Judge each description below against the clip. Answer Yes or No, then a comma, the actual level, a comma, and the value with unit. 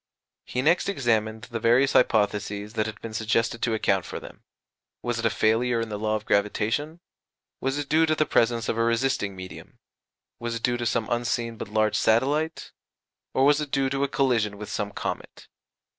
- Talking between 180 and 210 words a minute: Yes, average, 195 wpm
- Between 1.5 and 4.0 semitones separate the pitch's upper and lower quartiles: Yes, average, 3.6 semitones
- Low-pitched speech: Yes, low, 115 Hz